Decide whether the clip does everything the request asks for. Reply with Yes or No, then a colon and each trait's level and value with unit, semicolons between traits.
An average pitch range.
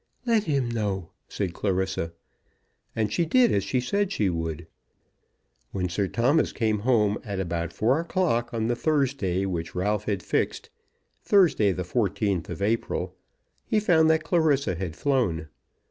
No: wide, 7.1 semitones